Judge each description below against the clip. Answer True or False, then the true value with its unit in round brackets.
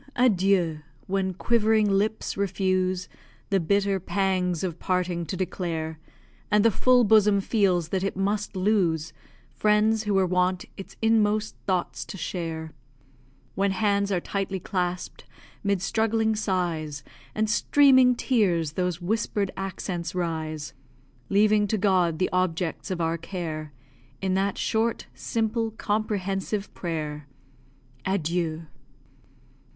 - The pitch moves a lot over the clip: False (3.2 semitones)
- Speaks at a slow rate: True (120 wpm)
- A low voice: False (190 Hz)